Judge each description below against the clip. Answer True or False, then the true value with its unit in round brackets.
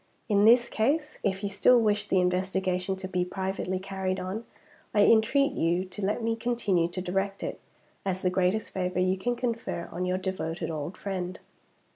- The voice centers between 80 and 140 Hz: False (190 Hz)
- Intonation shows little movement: False (3.0 semitones)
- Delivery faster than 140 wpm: True (180 wpm)